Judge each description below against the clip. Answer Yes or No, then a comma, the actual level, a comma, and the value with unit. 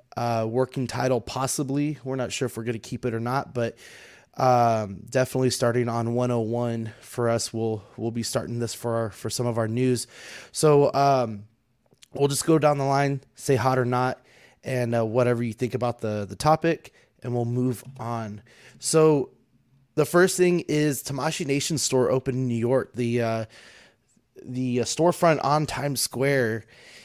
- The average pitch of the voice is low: Yes, low, 125 Hz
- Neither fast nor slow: Yes, average, 175 wpm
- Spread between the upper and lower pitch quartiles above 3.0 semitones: No, average, 2.7 semitones